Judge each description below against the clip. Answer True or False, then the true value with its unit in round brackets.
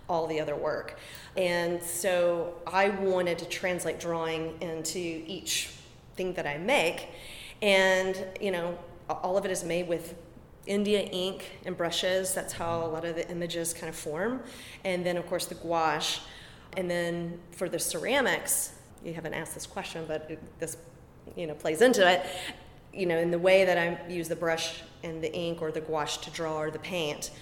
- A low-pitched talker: False (170 Hz)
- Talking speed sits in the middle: True (185 wpm)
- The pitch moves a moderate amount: False (2.0 semitones)